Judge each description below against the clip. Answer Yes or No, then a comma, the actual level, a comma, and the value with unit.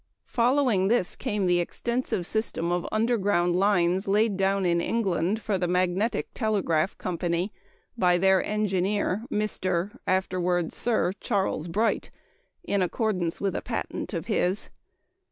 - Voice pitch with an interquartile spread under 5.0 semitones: Yes, average, 3.2 semitones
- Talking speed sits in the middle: No, slow, 130 wpm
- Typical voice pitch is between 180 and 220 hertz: Yes, high, 190 Hz